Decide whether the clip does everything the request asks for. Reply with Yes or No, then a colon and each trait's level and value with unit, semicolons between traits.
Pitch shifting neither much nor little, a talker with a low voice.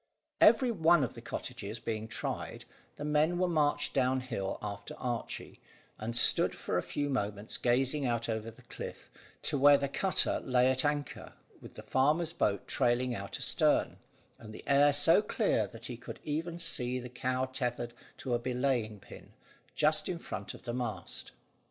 Yes: average, 3.8 semitones; low, 130 Hz